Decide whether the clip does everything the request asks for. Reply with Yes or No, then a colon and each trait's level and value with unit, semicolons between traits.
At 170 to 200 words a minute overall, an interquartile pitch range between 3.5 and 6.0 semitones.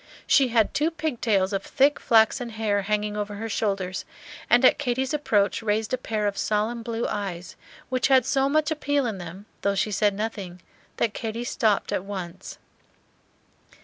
Yes: average, 175 wpm; average, 3.9 semitones